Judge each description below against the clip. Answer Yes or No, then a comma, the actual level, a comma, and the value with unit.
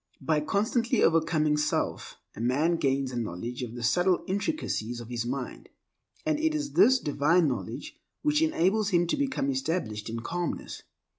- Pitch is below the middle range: No, medium, 165 Hz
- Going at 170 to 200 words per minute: No, average, 160 wpm